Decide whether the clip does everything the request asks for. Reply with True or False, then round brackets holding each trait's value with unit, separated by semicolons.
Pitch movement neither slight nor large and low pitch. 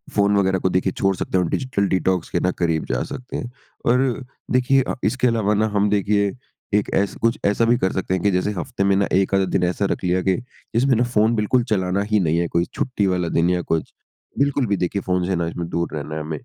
True (3.5 semitones; 100 Hz)